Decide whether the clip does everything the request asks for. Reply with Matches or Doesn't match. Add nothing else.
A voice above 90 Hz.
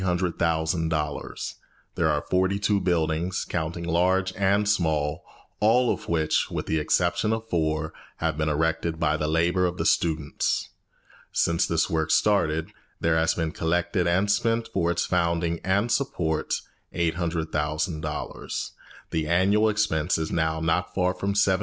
Doesn't match